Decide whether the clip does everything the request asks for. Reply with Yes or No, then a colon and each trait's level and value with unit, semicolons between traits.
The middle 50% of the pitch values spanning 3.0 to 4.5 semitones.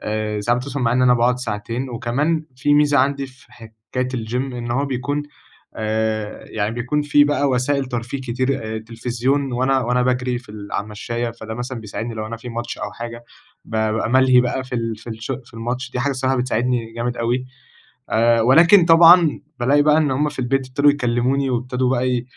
No: narrow, 2.5 semitones